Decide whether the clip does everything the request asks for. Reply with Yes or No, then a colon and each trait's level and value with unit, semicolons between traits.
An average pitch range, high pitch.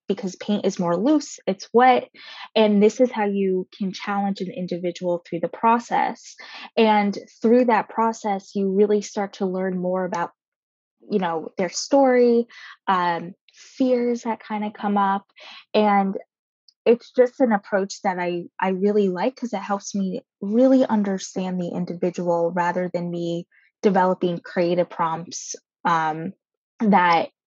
Yes: average, 3.6 semitones; high, 200 Hz